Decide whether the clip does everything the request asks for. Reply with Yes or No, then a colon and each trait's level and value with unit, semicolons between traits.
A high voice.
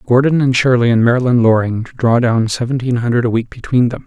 No: low, 120 Hz